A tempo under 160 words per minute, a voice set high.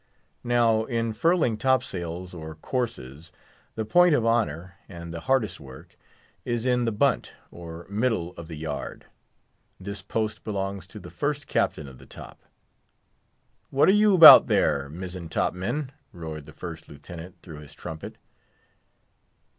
No: average, 150 wpm; very low, 95 Hz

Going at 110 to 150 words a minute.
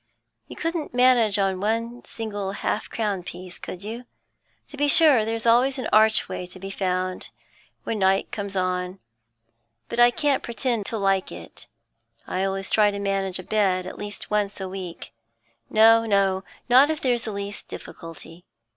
No: average, 165 wpm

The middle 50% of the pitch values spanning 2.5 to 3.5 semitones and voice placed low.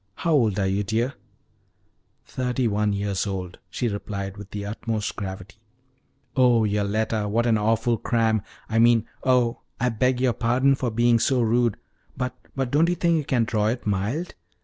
Yes: average, 3.1 semitones; low, 115 Hz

